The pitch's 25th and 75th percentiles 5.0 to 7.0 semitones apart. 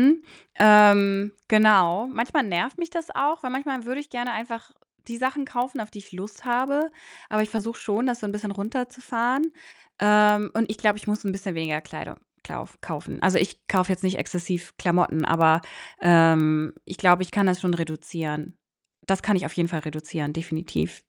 Yes: wide, 5.6 semitones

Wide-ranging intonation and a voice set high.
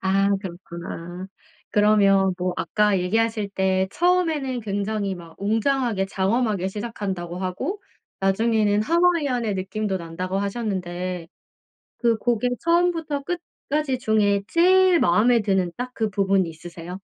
No: average, 4.5 semitones; high, 205 Hz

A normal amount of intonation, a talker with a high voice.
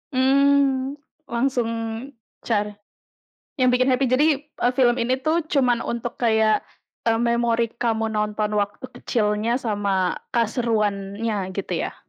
Yes: average, 3.3 semitones; high, 235 Hz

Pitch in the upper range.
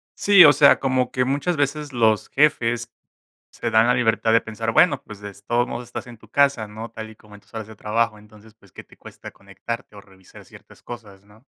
No: low, 115 Hz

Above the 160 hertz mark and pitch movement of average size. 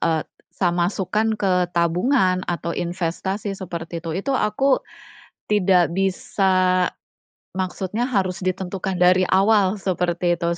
No: medium, 185 Hz; narrow, 1.9 semitones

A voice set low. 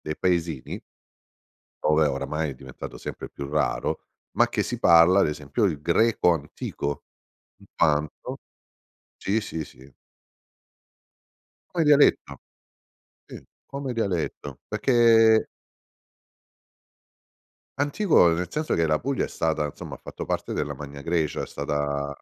Yes: very low, 80 Hz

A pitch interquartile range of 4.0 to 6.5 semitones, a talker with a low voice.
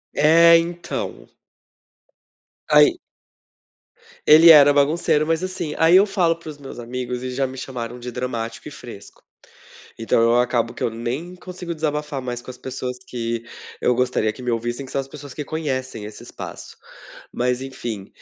Yes: average, 4.5 semitones; low, 130 Hz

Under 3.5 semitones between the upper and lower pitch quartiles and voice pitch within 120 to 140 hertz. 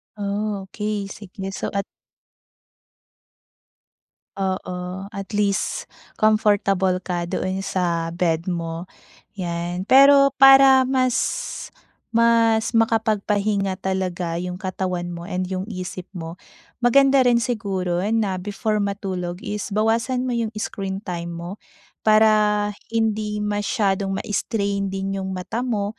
No: average, 3.0 semitones; high, 200 Hz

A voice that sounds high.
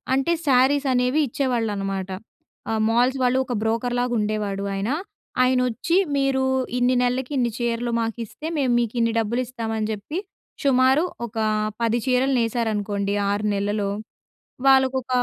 Yes: high, 240 Hz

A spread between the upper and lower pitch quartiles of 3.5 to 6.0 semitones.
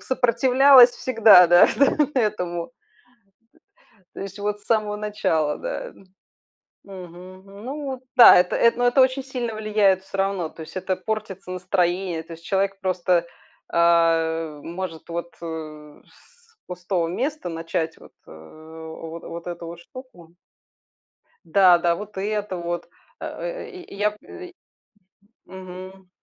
Yes: average, 4.1 semitones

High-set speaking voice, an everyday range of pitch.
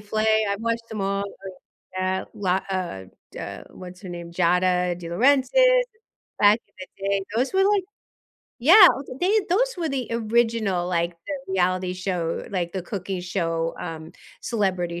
Yes: high, 195 Hz; average, 4.5 semitones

